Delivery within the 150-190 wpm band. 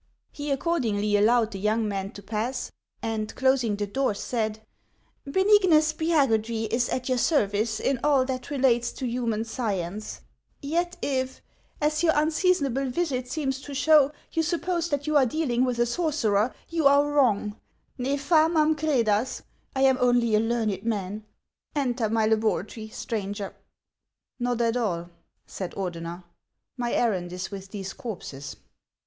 Yes: average, 155 wpm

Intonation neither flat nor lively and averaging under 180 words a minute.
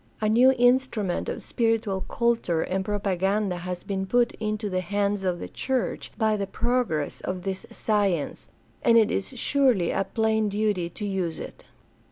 Yes: average, 3.2 semitones; average, 170 wpm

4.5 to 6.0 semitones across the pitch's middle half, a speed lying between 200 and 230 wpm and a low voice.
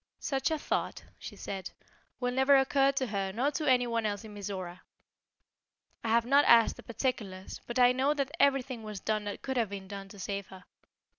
No: average, 4.9 semitones; fast, 205 wpm; high, 230 Hz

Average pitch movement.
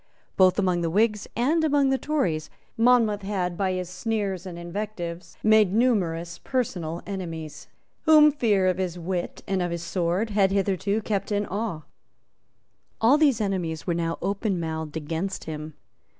Yes: average, 4.1 semitones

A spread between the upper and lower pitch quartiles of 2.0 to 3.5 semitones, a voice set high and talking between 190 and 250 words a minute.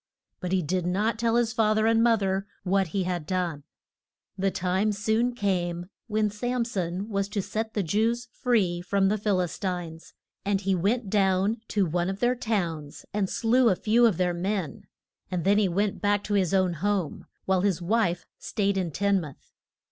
Yes: average, 3.0 semitones; high, 195 Hz; average, 195 wpm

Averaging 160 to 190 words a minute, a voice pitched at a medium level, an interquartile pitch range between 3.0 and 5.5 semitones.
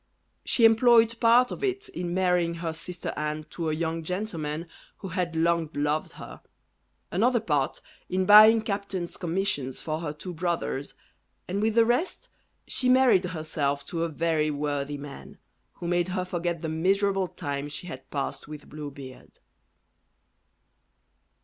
No: average, 150 wpm; medium, 170 Hz; average, 4.6 semitones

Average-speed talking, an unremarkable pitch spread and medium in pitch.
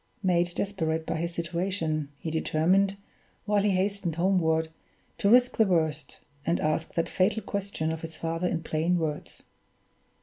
Yes: average, 155 wpm; average, 3.4 semitones; medium, 170 Hz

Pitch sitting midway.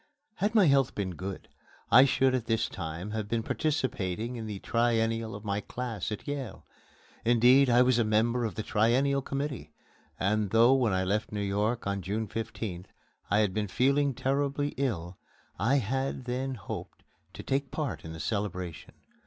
No: low, 115 Hz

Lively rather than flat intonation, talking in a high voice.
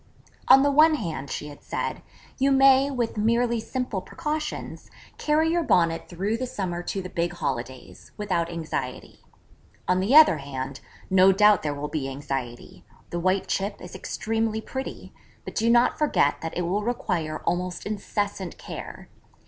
Yes: wide, 6.4 semitones; high, 195 Hz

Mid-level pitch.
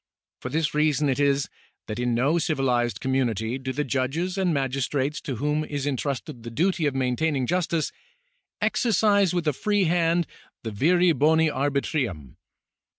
Yes: medium, 145 Hz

